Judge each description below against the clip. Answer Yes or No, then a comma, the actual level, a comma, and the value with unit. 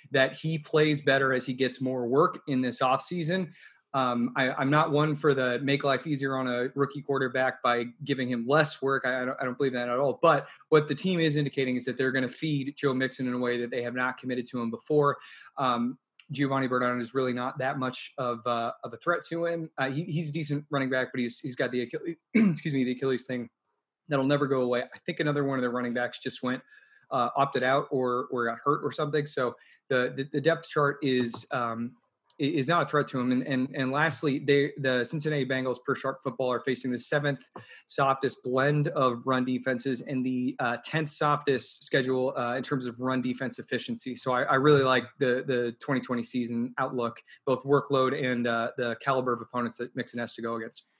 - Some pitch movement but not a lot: No, narrow, 2.3 semitones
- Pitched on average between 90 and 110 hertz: No, low, 130 Hz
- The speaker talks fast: Yes, fast, 225 wpm